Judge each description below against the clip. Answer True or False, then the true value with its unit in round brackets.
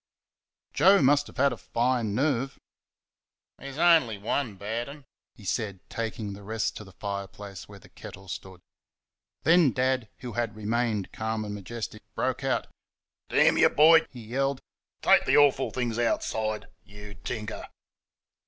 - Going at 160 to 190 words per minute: False (150 wpm)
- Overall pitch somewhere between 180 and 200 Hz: False (115 Hz)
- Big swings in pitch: False (4.4 semitones)